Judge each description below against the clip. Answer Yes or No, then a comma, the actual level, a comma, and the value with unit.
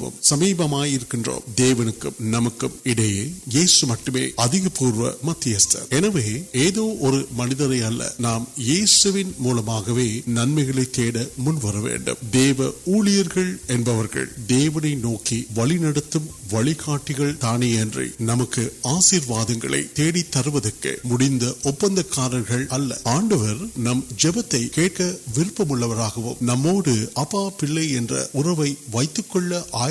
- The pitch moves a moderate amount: Yes, average, 5.0 semitones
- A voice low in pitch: Yes, low, 130 Hz